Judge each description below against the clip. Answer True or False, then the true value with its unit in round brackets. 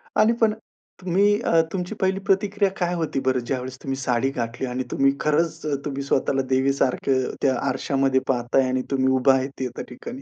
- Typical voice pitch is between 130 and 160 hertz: True (135 Hz)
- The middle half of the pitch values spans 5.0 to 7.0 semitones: True (5.4 semitones)